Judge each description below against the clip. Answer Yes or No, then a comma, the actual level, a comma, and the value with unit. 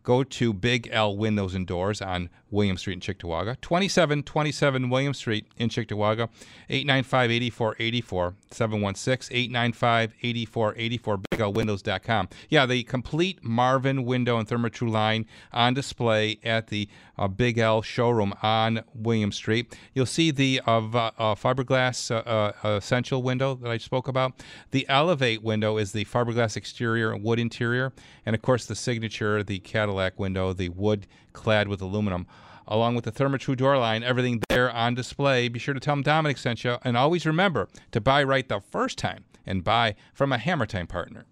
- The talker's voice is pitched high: No, low, 115 Hz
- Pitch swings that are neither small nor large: Yes, average, 3.3 semitones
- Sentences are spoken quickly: No, average, 160 wpm